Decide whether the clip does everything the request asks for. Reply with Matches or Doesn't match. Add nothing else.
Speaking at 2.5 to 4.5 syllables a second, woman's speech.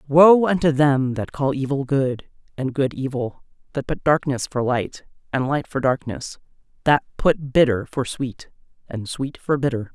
Matches